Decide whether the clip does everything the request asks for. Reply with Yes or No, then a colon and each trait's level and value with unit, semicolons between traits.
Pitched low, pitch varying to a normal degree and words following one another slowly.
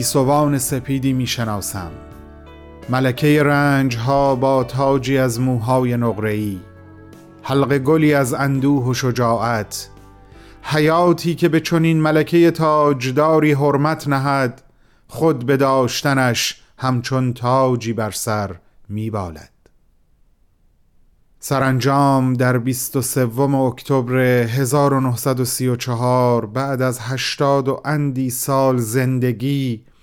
Yes: low, 130 Hz; average, 3.0 semitones; slow, 95 wpm